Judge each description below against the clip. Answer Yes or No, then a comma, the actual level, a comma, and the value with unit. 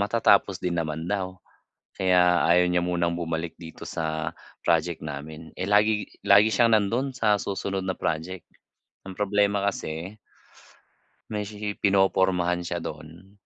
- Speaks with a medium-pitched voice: No, very low, 95 Hz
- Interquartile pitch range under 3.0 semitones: No, average, 3.3 semitones